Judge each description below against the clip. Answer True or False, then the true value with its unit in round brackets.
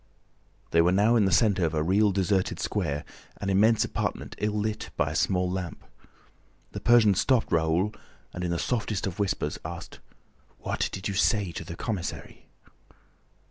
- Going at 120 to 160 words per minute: False (170 wpm)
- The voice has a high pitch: False (95 Hz)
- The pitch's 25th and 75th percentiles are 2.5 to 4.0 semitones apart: True (3.4 semitones)